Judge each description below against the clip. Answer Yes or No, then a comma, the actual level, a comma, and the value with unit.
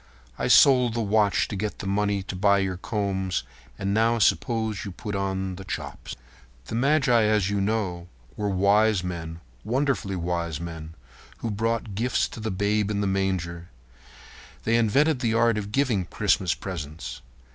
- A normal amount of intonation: Yes, average, 3.3 semitones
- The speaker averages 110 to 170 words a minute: Yes, average, 155 wpm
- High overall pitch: No, low, 100 Hz